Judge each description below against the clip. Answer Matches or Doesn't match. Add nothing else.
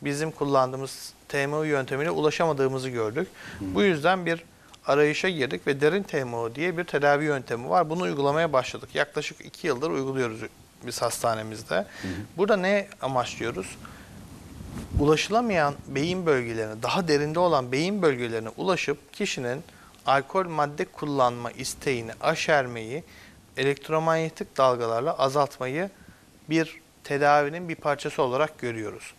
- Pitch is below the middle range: Doesn't match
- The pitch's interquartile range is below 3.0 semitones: Doesn't match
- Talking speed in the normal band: Matches